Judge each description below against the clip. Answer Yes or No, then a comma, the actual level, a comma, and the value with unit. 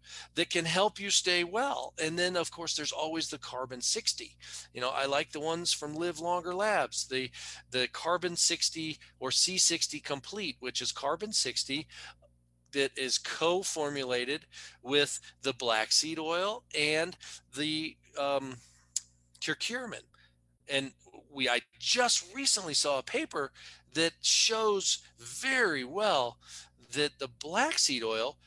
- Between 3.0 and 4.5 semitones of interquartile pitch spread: No, average, 5.1 semitones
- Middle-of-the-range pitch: Yes, medium, 150 Hz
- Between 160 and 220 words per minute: No, slow, 135 wpm